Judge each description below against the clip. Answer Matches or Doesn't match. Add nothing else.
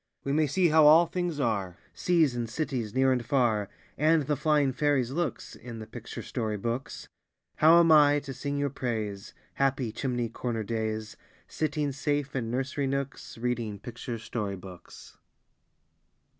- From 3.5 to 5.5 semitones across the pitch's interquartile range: Matches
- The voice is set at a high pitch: Doesn't match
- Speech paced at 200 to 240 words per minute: Doesn't match